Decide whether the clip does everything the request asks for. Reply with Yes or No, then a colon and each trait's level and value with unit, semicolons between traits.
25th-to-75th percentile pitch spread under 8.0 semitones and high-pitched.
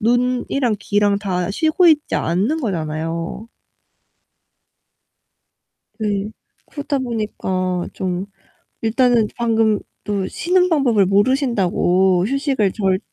Yes: average, 5.1 semitones; high, 215 Hz